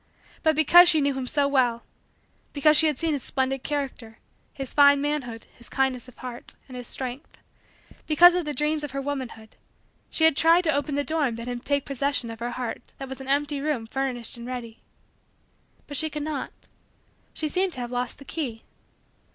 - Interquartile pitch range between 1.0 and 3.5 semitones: Yes, average, 3.2 semitones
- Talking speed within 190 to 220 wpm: Yes, fast, 205 wpm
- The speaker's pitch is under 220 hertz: No, very high, 275 Hz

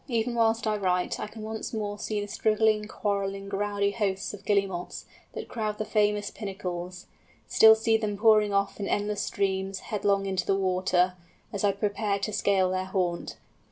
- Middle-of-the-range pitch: No, high, 205 Hz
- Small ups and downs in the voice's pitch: Yes, narrow, 1.7 semitones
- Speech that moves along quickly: No, average, 175 wpm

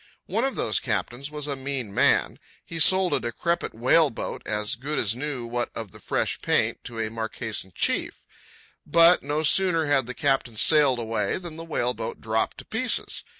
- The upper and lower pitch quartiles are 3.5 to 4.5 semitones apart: No, average, 5.3 semitones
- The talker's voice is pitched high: No, low, 130 Hz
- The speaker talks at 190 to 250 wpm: Yes, average, 195 wpm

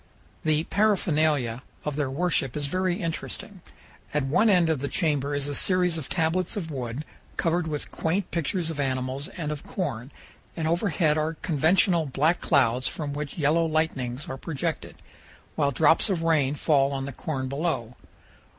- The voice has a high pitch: No, medium, 155 Hz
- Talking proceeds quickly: No, average, 165 wpm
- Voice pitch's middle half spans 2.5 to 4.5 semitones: Yes, average, 3.3 semitones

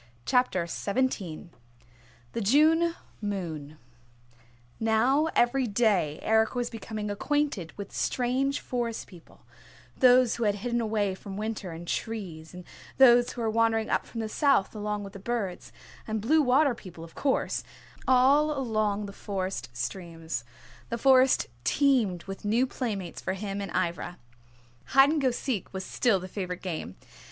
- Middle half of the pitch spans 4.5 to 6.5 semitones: Yes, average, 4.9 semitones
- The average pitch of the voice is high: Yes, high, 220 Hz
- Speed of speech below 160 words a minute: Yes, average, 150 wpm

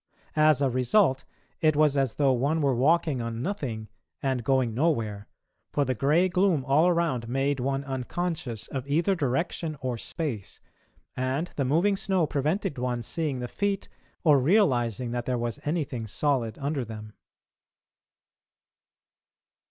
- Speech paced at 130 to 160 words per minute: Yes, average, 145 wpm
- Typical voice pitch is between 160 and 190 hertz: No, low, 135 Hz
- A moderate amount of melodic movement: Yes, average, 4.4 semitones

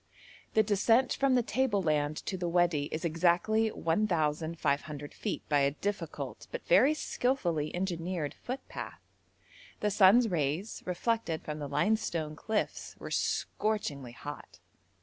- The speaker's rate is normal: No, slow, 130 wpm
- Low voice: No, medium, 175 Hz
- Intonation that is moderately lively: No, wide, 6.1 semitones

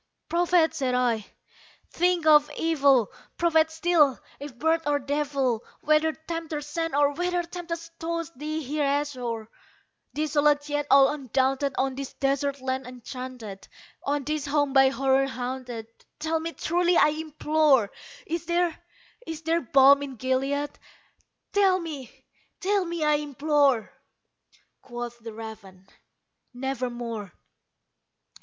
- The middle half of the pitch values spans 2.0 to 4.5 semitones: Yes, average, 3.5 semitones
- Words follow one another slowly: Yes, slow, 125 wpm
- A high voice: Yes, very high, 290 Hz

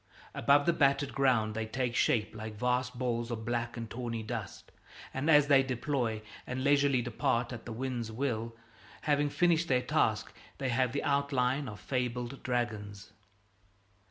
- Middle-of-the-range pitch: No, low, 125 Hz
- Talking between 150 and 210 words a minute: Yes, average, 155 wpm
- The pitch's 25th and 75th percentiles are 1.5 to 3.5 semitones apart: Yes, average, 3.0 semitones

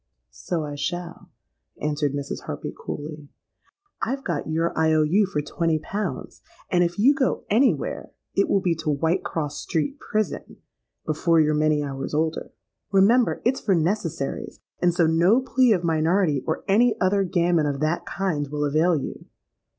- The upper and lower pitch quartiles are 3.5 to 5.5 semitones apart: Yes, average, 4.4 semitones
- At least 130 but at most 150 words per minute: No, average, 165 wpm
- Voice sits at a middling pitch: Yes, medium, 165 Hz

